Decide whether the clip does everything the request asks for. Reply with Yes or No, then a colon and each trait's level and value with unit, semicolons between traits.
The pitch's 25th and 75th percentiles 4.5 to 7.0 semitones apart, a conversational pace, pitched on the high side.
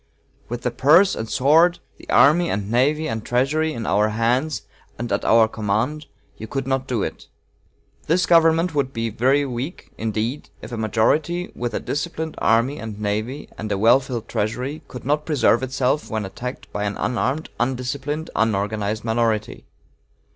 No: average, 5.0 semitones; average, 165 wpm; low, 125 Hz